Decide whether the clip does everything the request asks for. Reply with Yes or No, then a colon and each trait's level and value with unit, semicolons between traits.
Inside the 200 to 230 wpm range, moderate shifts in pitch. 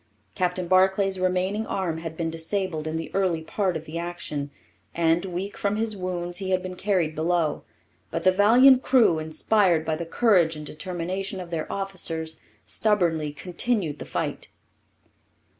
No: average, 160 wpm; average, 3.2 semitones